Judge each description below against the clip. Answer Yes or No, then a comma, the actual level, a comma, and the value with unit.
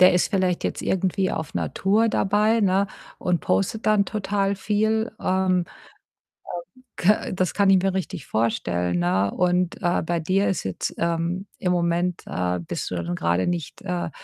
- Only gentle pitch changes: No, average, 3.2 semitones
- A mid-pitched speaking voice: Yes, medium, 180 Hz